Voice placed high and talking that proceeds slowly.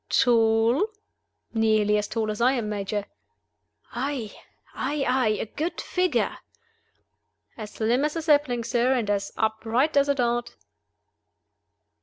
Yes: high, 235 Hz; slow, 130 wpm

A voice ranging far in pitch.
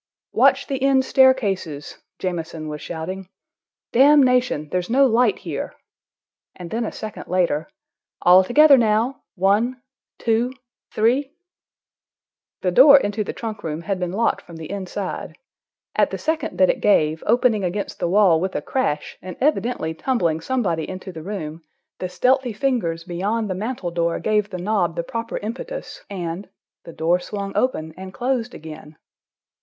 Yes: wide, 6.2 semitones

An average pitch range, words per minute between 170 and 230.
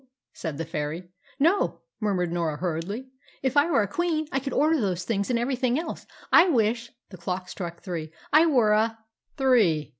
No: wide, 7.4 semitones; average, 185 wpm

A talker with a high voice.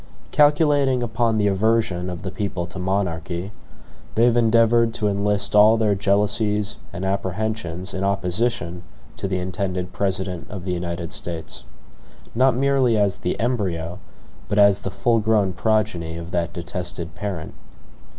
No: low, 100 Hz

